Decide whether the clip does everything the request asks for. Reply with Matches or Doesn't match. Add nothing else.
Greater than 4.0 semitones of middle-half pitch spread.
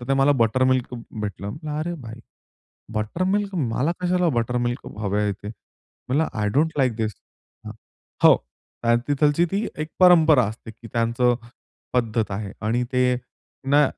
Matches